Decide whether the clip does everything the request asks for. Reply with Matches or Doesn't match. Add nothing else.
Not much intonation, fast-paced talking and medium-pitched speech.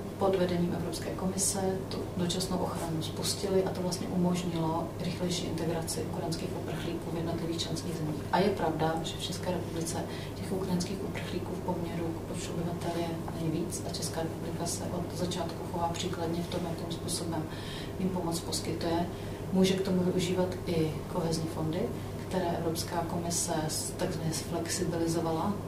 Doesn't match